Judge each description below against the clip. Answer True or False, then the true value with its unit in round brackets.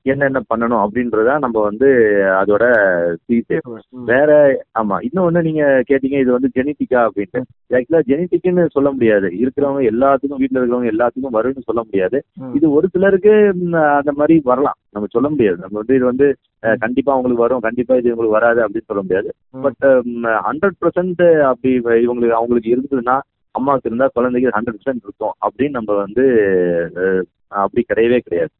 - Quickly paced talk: True (145 wpm)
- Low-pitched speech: True (125 Hz)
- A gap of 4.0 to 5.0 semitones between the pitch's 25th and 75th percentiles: False (3.6 semitones)